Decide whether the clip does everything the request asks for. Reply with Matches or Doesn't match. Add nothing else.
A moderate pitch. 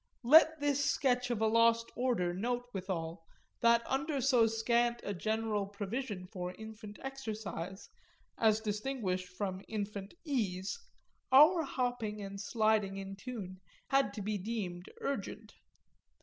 Doesn't match